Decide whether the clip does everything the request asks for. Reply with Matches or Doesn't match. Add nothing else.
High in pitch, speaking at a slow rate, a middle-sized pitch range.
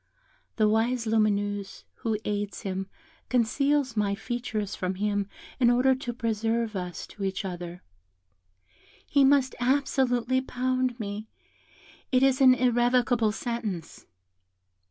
Matches